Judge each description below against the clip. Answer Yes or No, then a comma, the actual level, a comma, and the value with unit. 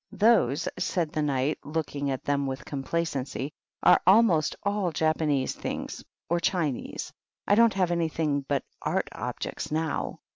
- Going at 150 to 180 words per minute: No, average, 140 wpm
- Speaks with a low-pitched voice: No, medium, 155 Hz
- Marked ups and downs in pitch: No, average, 3.5 semitones